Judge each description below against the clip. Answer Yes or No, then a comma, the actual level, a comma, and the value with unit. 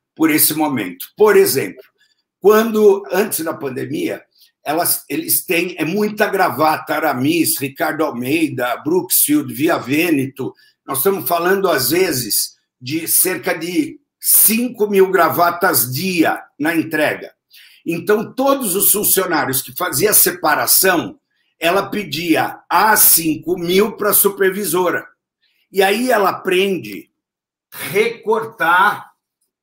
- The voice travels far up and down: Yes, wide, 8.2 semitones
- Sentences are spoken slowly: Yes, slow, 115 wpm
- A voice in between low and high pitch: No, high, 195 Hz